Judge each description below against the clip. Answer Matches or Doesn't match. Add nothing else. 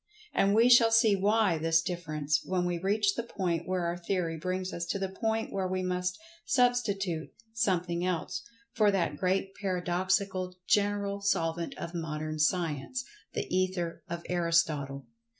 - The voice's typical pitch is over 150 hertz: Matches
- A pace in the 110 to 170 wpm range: Matches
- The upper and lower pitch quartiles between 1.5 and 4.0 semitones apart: Matches